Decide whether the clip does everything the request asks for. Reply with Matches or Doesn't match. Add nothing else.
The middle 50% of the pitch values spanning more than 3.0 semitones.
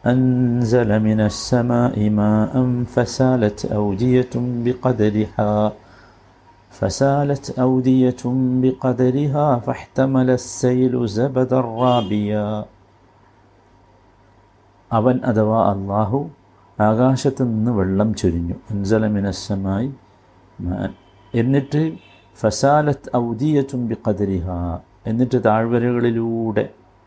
Matches